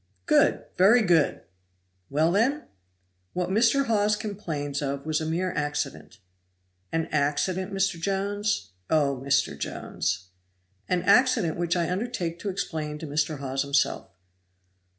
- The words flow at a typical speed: No, slow, 130 wpm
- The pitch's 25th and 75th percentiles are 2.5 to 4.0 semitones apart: No, wide, 5.4 semitones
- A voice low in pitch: No, medium, 170 Hz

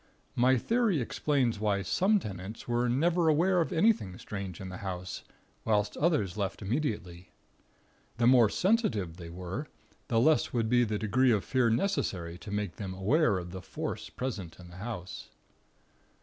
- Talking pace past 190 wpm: No, average, 165 wpm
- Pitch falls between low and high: No, low, 110 Hz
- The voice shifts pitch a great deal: Yes, wide, 6.6 semitones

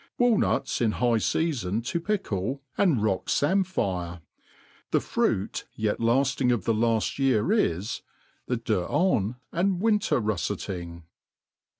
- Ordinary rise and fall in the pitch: No, wide, 8.7 semitones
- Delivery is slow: Yes, slow, 120 wpm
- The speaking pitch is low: Yes, low, 115 Hz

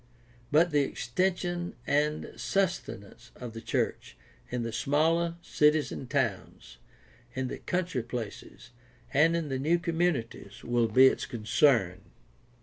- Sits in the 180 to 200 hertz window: No, medium, 140 Hz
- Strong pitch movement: Yes, wide, 5.9 semitones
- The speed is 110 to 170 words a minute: Yes, average, 140 wpm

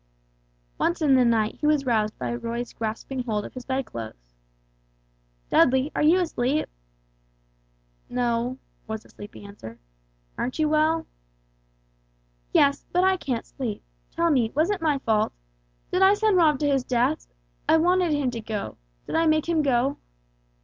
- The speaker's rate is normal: Yes, average, 155 wpm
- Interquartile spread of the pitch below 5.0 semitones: No, wide, 5.4 semitones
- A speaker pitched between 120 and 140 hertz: No, very high, 265 Hz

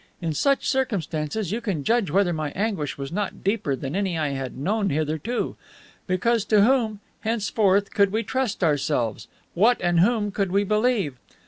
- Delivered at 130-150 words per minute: No, average, 165 wpm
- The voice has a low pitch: No, high, 195 Hz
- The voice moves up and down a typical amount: No, wide, 5.9 semitones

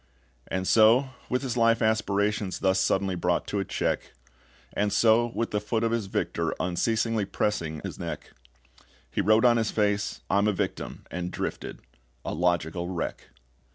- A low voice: Yes, low, 105 Hz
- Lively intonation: No, average, 3.4 semitones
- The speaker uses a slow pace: No, average, 160 wpm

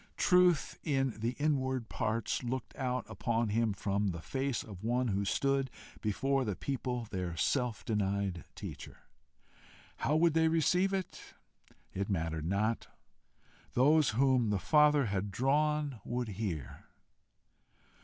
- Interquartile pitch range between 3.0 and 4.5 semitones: No, wide, 5.4 semitones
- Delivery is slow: Yes, slow, 130 wpm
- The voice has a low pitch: Yes, low, 120 Hz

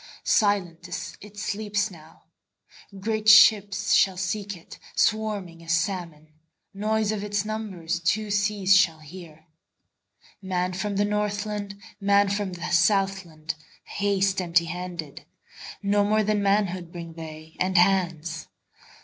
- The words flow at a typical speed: No, slow, 95 wpm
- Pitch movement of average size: Yes, average, 3.3 semitones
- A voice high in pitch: Yes, high, 195 Hz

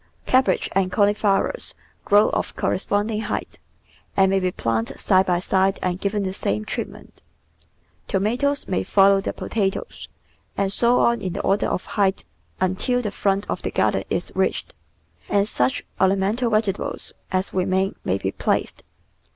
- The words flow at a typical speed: Yes, average, 160 wpm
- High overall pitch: Yes, high, 195 Hz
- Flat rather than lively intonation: Yes, narrow, 1.9 semitones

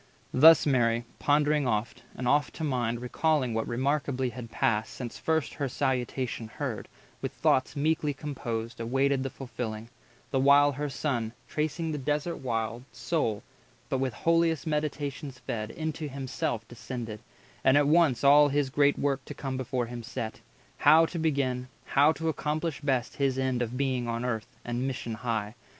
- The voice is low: Yes, low, 130 Hz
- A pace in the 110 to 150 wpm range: No, average, 165 wpm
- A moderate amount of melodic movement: Yes, average, 3.5 semitones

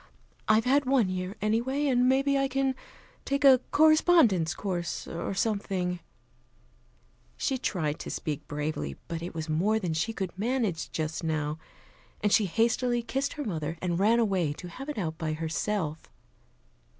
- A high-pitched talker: Yes, high, 200 Hz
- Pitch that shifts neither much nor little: No, wide, 7.6 semitones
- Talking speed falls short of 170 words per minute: Yes, average, 160 wpm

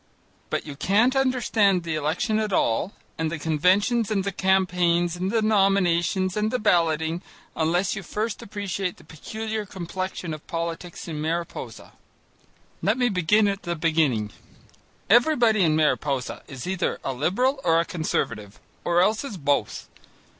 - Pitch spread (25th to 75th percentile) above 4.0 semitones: Yes, average, 4.6 semitones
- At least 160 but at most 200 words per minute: No, average, 150 wpm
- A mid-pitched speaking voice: Yes, medium, 180 Hz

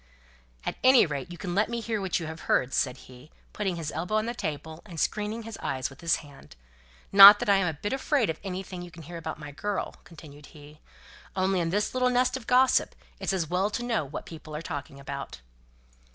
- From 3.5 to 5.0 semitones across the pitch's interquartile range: No, wide, 5.6 semitones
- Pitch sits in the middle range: Yes, medium, 175 Hz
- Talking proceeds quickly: Yes, fast, 220 wpm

